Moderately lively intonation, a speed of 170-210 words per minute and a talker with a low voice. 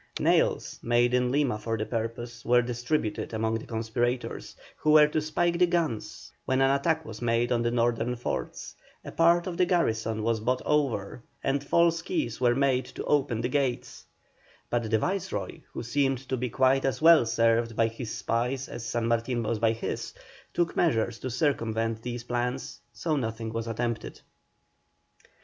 Yes: average, 3.4 semitones; average, 175 wpm; low, 120 Hz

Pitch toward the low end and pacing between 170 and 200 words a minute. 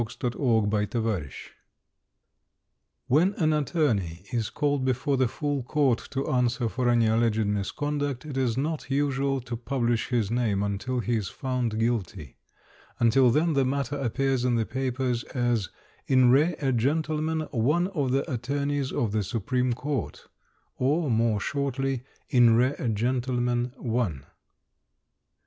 No: low, 125 Hz; average, 145 wpm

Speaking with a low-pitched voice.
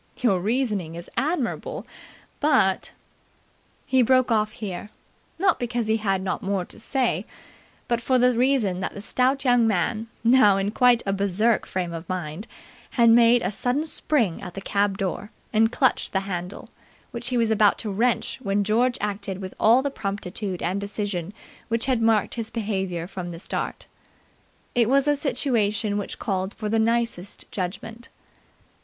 No: high, 215 Hz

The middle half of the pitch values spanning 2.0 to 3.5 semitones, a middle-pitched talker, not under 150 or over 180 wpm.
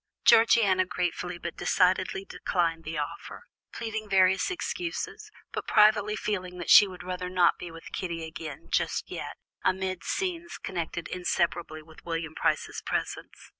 No: average, 3.2 semitones; medium, 180 Hz; average, 140 wpm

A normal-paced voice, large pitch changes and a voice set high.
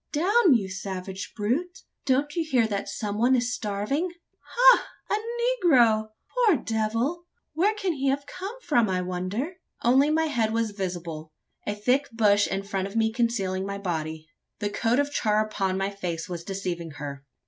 Yes: average, 170 wpm; wide, 6.9 semitones; high, 220 Hz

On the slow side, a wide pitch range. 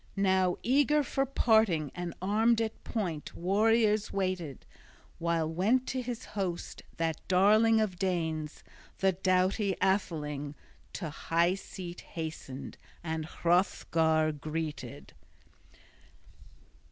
No: slow, 105 wpm; average, 4.7 semitones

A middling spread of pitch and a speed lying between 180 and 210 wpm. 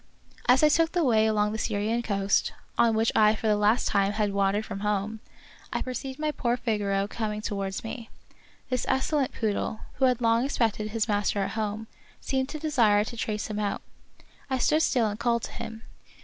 Yes: average, 3.1 semitones; average, 200 wpm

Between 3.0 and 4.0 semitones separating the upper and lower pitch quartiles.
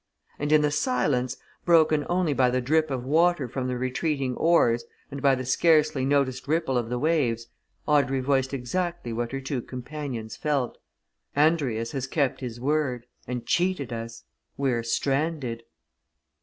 Yes: average, 3.6 semitones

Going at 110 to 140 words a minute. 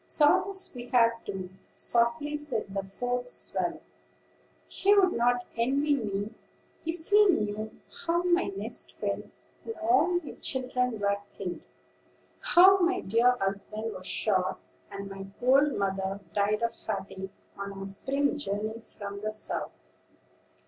Yes: slow, 135 wpm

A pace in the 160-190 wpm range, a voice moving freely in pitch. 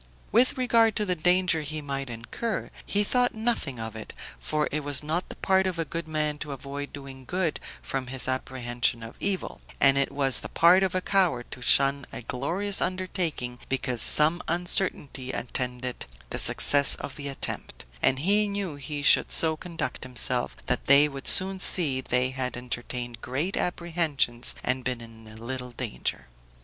Yes: average, 175 wpm; wide, 5.8 semitones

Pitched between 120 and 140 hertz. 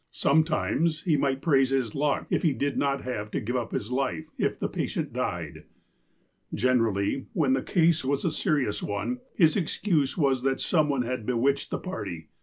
Yes: low, 135 Hz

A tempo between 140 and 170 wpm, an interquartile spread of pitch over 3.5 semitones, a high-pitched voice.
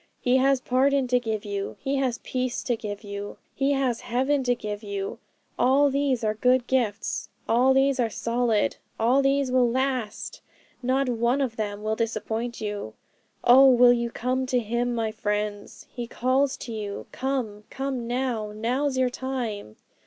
No: average, 165 wpm; average, 3.2 semitones; high, 245 Hz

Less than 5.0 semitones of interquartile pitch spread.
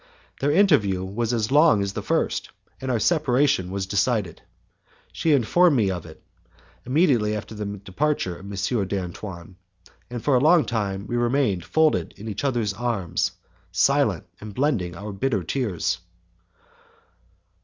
No: wide, 5.6 semitones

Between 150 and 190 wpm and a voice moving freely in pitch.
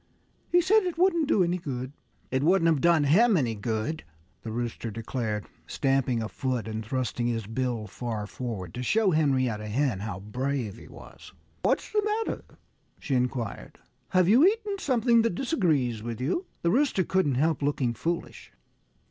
Yes: average, 165 wpm; wide, 8.4 semitones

